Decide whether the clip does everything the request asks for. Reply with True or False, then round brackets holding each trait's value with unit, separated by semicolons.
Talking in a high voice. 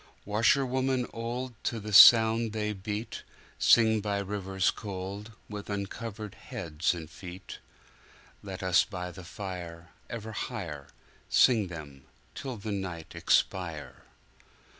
False (100 Hz)